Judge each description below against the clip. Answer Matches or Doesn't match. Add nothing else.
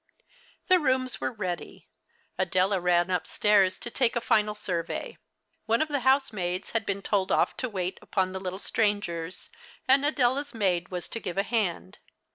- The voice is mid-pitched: Doesn't match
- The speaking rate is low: Doesn't match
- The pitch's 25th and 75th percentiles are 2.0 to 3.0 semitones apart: Doesn't match